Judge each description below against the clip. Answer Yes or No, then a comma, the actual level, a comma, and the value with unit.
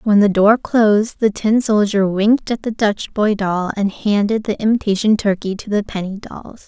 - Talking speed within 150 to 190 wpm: No, average, 200 wpm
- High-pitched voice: Yes, high, 210 Hz